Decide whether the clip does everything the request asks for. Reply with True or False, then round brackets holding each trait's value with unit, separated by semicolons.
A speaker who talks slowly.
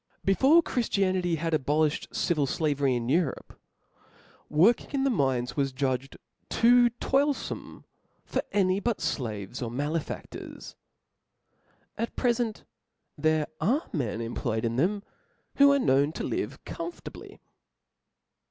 True (130 wpm)